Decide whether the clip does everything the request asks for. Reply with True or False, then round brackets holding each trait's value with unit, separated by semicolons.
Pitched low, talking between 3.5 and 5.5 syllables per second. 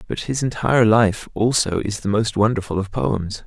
True (105 Hz; 5.0 syllables/s)